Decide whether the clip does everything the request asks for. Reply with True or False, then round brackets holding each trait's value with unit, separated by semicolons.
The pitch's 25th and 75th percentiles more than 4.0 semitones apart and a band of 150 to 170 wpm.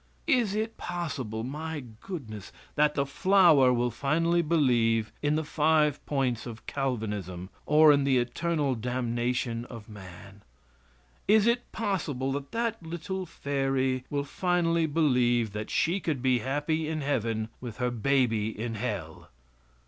False (5.2 semitones; 140 wpm)